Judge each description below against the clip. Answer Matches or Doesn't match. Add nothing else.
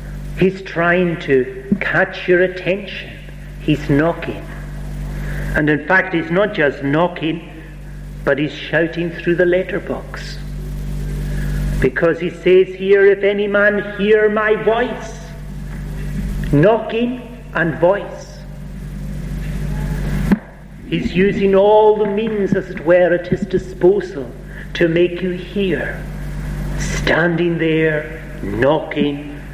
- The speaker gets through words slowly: Matches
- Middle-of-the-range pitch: Matches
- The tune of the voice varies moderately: Matches